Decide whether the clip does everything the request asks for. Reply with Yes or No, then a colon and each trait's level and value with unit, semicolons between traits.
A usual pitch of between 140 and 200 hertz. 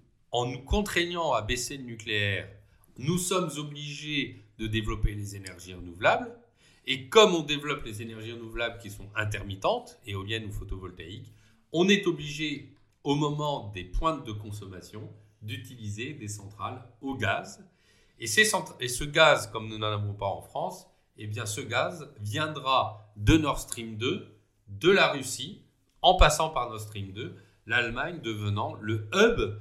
No: low, 110 Hz